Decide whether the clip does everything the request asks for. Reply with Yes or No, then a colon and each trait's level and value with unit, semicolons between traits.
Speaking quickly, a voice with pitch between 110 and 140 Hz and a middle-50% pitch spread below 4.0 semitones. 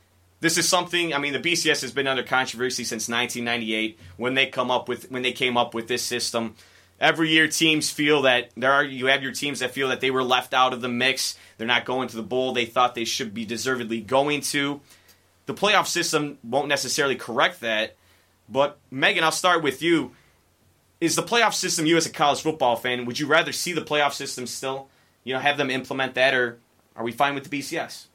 Yes: fast, 220 wpm; low, 130 Hz; average, 3.2 semitones